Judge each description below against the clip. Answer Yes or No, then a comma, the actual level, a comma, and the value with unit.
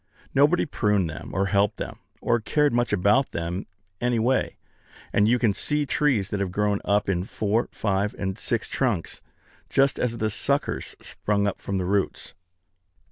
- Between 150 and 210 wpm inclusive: Yes, average, 170 wpm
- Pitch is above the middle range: No, low, 105 Hz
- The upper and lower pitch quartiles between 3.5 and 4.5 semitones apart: Yes, average, 3.8 semitones